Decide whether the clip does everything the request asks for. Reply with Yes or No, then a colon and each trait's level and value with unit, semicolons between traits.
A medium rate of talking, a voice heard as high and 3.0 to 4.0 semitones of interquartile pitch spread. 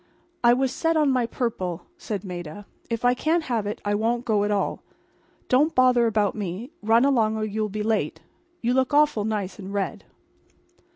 Yes: average, 185 wpm; high, 220 Hz; average, 3.6 semitones